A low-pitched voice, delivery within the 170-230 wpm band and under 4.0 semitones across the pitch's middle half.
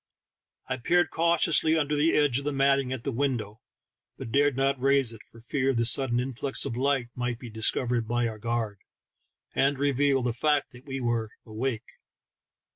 Yes: low, 130 Hz; average, 180 wpm; average, 3.0 semitones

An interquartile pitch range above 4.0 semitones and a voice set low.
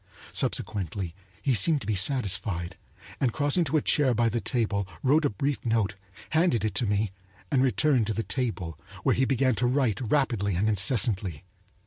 Yes: average, 4.9 semitones; low, 115 Hz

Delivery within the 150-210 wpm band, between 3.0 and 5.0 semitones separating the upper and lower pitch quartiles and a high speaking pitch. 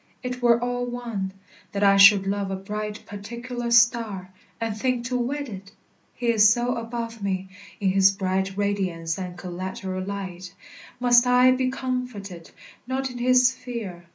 Yes: average, 155 wpm; average, 4.2 semitones; high, 215 Hz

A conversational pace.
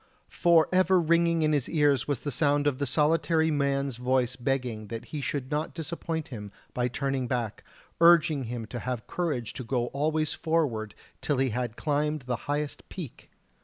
Yes: average, 175 wpm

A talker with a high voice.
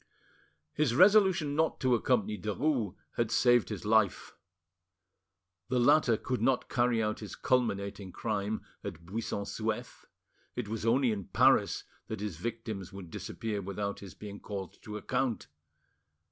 No: low, 110 Hz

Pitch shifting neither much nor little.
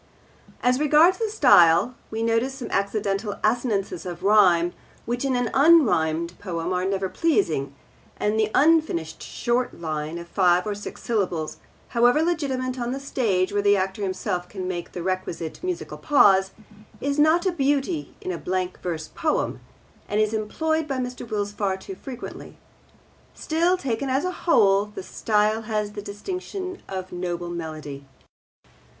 No: wide, 6.8 semitones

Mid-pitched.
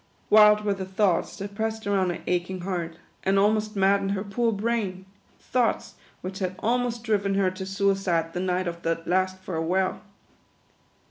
No: high, 195 Hz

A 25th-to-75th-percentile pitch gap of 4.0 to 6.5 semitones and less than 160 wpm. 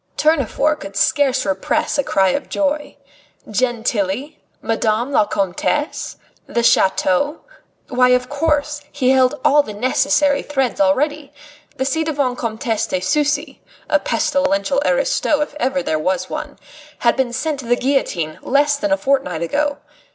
Yes: average, 4.3 semitones; average, 145 wpm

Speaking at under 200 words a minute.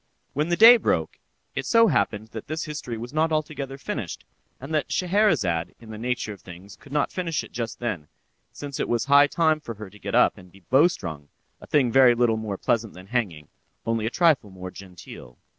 No: fast, 205 wpm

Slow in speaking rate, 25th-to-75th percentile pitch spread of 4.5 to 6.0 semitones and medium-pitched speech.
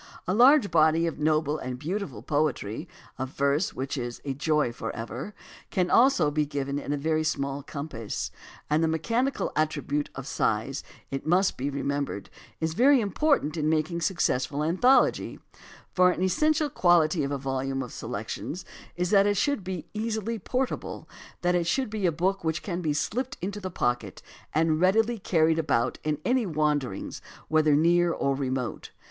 No: average, 175 wpm; average, 5.1 semitones; medium, 155 Hz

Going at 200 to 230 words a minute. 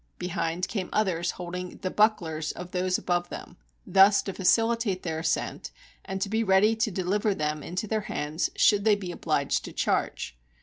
No: average, 175 wpm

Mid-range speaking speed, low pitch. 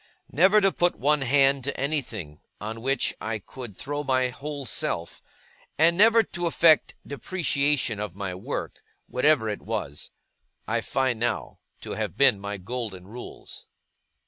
Yes: average, 145 wpm; low, 130 Hz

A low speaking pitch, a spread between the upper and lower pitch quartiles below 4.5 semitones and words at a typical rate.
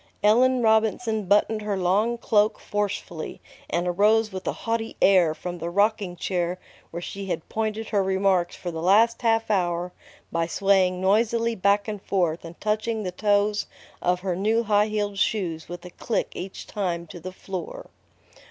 No: high, 200 Hz; average, 3.3 semitones; average, 170 wpm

